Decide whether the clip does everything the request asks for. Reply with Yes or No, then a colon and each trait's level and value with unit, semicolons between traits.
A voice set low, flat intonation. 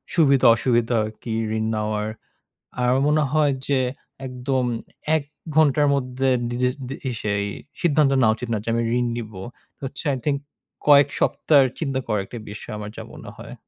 No: low, 125 Hz; average, 3.7 semitones